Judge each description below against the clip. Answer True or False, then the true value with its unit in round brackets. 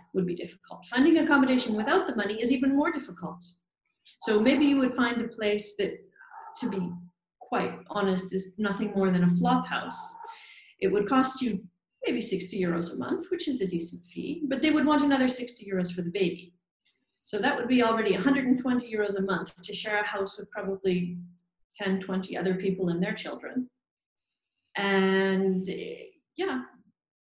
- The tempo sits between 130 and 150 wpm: False (175 wpm)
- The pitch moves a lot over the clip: True (6.5 semitones)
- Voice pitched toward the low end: False (210 Hz)